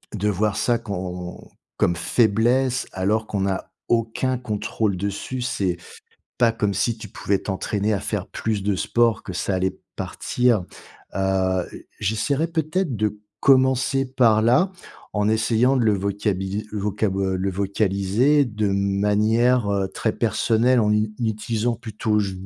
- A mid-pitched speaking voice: No, low, 105 Hz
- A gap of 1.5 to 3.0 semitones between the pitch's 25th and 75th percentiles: No, average, 3.4 semitones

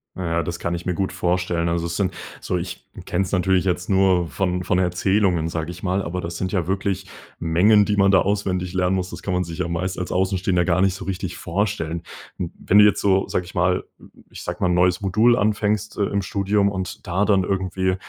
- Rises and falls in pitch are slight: Yes, narrow, 1.7 semitones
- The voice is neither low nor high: No, very low, 90 Hz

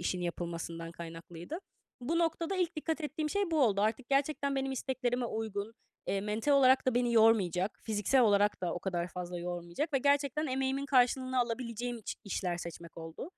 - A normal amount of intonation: No, wide, 7.3 semitones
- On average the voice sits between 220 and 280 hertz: Yes, high, 235 Hz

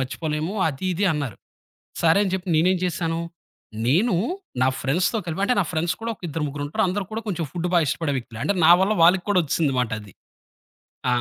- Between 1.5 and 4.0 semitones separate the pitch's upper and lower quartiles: No, average, 4.4 semitones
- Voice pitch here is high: No, medium, 165 Hz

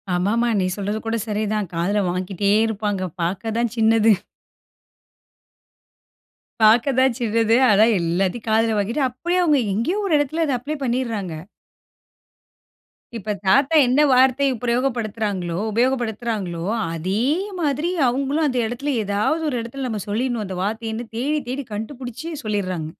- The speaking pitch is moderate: No, high, 225 Hz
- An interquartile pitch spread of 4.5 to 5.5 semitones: No, average, 4.0 semitones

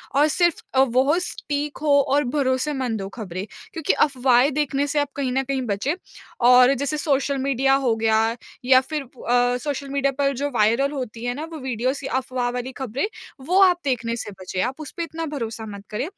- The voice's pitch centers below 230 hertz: No, very high, 265 Hz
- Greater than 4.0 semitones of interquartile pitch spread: No, average, 2.8 semitones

